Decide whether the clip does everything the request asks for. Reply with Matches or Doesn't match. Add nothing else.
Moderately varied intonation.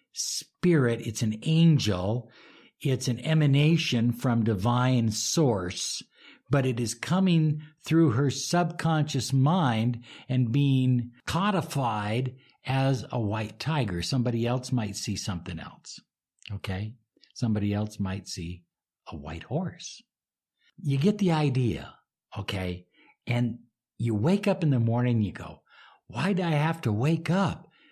Doesn't match